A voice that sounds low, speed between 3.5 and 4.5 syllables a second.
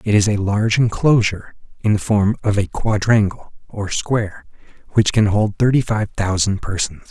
No: low, 105 Hz; 4.9 syllables/s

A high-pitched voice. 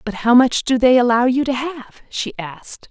Yes: high, 245 Hz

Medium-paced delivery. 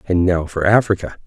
Yes: average, 190 wpm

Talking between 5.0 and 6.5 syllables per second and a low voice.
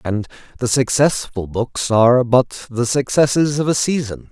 No: 4.4 syllables/s; low, 125 Hz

